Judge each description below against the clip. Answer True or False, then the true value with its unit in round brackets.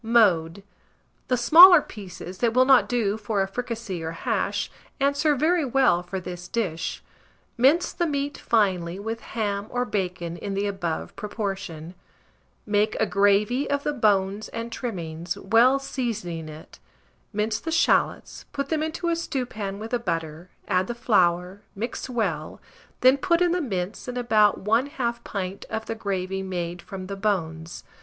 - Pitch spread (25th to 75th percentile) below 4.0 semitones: False (5.1 semitones)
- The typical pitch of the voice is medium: False (210 Hz)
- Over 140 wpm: True (160 wpm)